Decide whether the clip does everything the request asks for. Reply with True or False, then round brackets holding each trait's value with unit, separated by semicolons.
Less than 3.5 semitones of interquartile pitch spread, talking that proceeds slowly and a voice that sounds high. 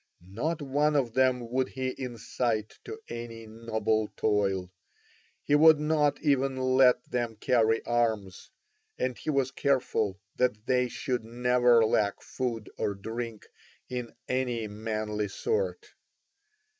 False (3.0 semitones; 125 wpm; 120 Hz)